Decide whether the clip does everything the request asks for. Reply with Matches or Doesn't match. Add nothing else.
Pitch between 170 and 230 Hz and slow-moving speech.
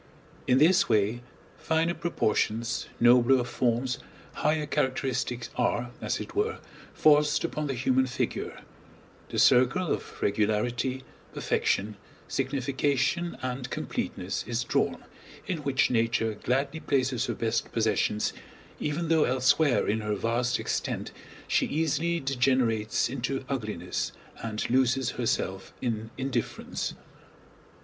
Doesn't match